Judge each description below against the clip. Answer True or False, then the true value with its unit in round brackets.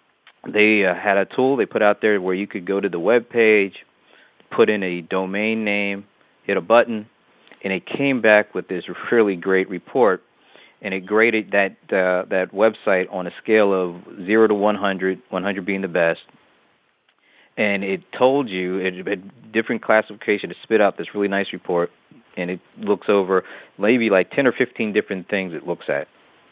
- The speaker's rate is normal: True (185 wpm)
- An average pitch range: False (2.3 semitones)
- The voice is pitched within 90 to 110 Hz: True (100 Hz)